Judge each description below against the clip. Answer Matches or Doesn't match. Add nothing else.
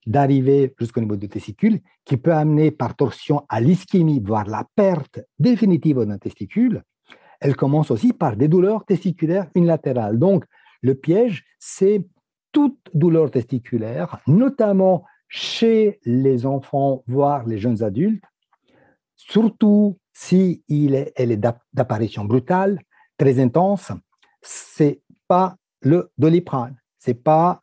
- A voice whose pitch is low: Doesn't match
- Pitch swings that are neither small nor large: Doesn't match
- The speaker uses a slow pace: Matches